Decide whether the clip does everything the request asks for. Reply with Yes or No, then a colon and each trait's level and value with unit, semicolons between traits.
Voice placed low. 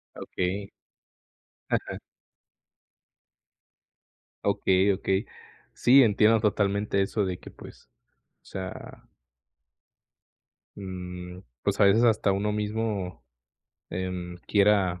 Yes: low, 100 Hz